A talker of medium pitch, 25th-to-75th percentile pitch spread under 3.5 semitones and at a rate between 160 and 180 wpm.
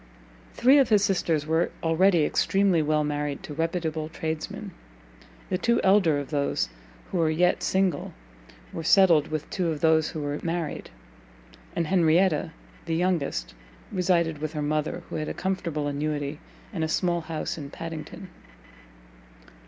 No: medium, 160 Hz; average, 2.9 semitones; average, 150 wpm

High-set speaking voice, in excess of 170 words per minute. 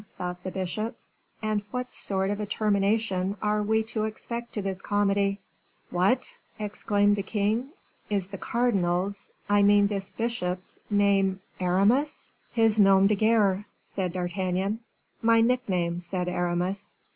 No: high, 200 Hz; slow, 135 wpm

